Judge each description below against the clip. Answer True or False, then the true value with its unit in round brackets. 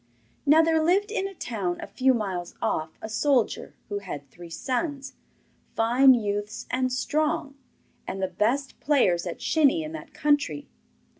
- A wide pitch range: True (6.6 semitones)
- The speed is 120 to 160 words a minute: True (155 wpm)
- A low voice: False (255 Hz)